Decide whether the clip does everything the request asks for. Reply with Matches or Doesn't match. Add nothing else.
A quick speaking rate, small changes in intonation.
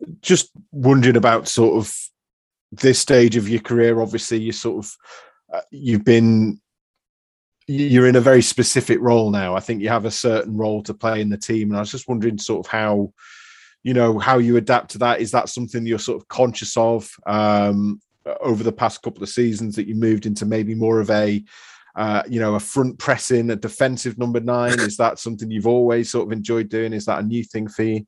Matches